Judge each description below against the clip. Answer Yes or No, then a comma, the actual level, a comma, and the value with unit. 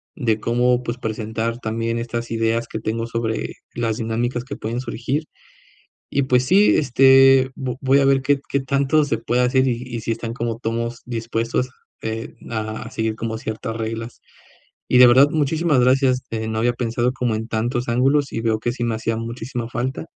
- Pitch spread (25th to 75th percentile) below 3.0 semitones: Yes, narrow, 2.4 semitones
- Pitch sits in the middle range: No, low, 120 Hz